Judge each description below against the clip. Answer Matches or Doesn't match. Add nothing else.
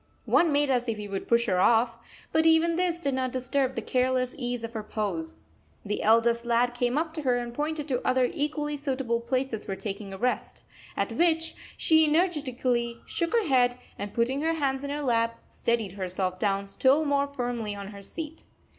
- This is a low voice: Doesn't match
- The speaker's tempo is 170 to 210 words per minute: Matches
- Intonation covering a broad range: Doesn't match